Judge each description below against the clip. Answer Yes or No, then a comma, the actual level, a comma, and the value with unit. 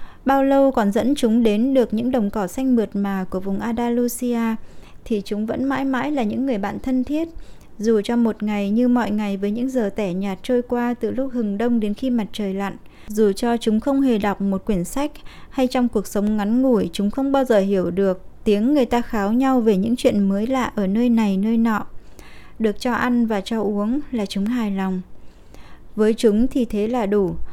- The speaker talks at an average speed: Yes, average, 220 wpm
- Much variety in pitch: No, average, 3.3 semitones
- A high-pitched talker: Yes, high, 225 Hz